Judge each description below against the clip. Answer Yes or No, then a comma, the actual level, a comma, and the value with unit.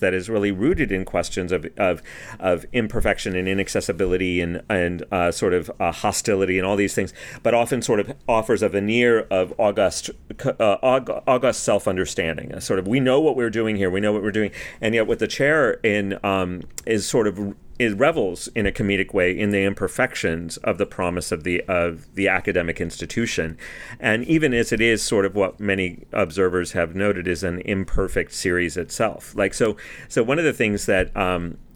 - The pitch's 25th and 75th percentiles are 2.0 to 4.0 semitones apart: Yes, average, 2.9 semitones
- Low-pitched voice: Yes, very low, 95 Hz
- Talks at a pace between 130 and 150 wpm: No, average, 195 wpm